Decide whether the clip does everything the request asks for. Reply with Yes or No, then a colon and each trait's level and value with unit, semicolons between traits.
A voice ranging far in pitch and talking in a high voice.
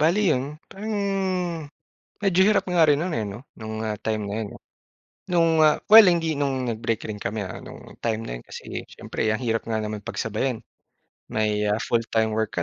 No: wide, 6.9 semitones; low, 115 Hz